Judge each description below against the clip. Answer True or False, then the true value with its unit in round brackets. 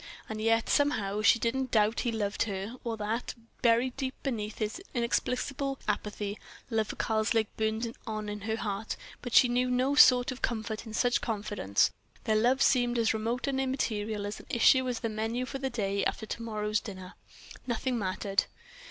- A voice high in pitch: True (225 Hz)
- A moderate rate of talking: True (175 wpm)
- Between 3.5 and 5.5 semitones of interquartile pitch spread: False (2.8 semitones)